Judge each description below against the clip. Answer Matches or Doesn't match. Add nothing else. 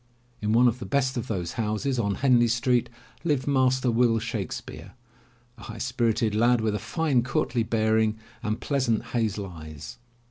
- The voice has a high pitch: Doesn't match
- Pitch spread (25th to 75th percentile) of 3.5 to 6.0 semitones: Doesn't match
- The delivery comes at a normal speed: Matches